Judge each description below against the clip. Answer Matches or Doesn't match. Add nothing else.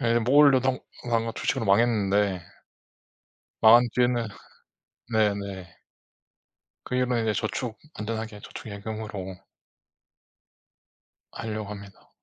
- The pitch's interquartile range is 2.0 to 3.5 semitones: Matches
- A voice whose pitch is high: Doesn't match